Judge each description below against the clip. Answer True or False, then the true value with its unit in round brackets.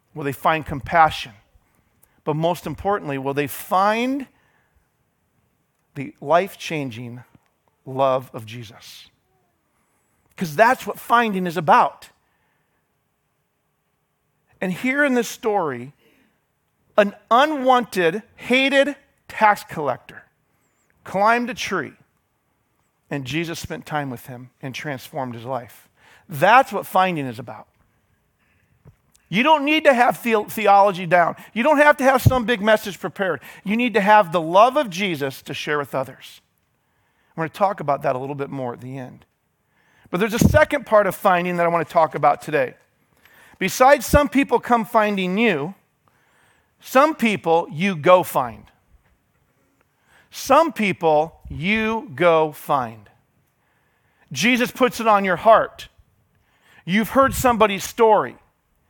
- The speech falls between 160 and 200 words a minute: False (135 wpm)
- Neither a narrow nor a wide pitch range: False (8.3 semitones)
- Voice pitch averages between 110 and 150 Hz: False (175 Hz)